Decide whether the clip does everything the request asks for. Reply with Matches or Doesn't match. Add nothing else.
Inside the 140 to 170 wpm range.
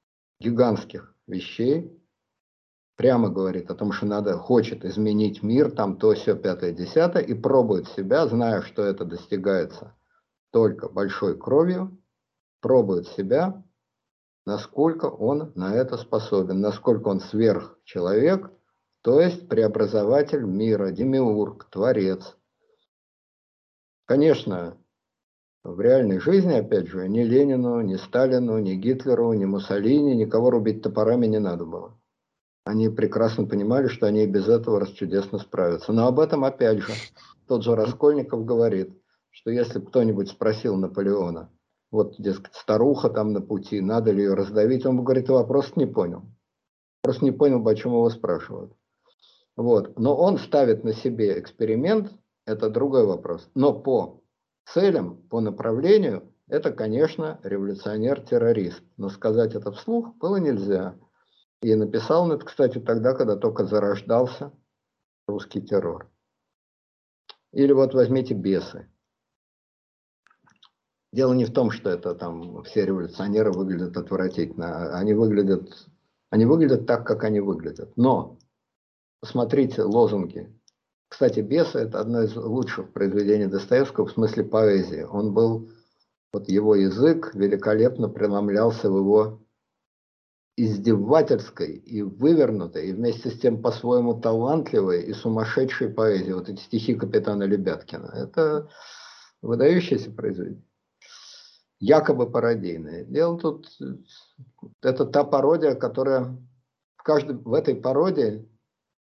Doesn't match